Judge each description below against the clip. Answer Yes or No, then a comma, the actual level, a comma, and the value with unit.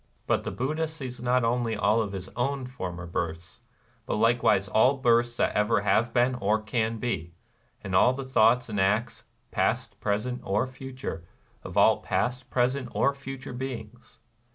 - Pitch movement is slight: No, average, 3.3 semitones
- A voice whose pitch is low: Yes, low, 120 Hz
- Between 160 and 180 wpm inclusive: Yes, average, 175 wpm